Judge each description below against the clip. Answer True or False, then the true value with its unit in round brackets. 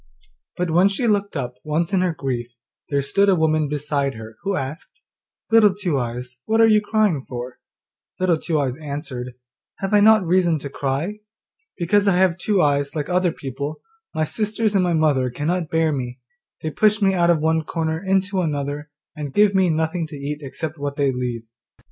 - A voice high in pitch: False (160 Hz)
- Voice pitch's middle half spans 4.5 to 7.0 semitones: True (5.1 semitones)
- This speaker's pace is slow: False (190 wpm)